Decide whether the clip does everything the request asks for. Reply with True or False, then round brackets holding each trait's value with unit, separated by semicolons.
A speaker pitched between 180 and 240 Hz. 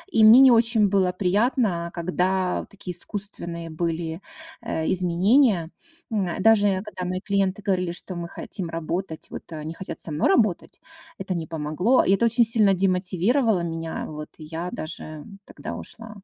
True (185 Hz)